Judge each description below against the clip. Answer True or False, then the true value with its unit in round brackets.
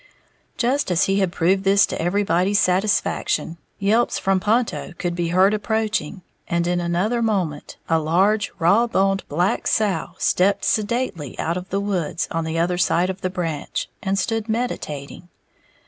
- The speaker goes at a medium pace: True (160 wpm)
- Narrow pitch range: False (3.3 semitones)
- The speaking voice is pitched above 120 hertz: True (190 Hz)